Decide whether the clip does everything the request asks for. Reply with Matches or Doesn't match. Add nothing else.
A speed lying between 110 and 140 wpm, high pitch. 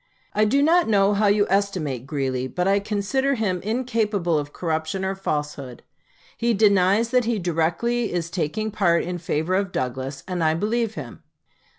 Doesn't match